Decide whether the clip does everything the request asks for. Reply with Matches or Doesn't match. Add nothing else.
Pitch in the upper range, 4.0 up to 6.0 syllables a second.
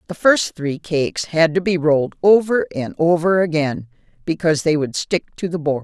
Doesn't match